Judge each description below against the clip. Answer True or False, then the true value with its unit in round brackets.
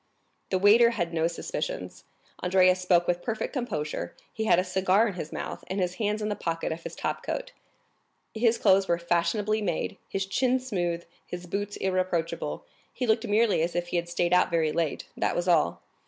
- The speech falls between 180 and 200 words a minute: True (195 wpm)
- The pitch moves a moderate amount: True (3.7 semitones)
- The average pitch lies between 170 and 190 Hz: True (185 Hz)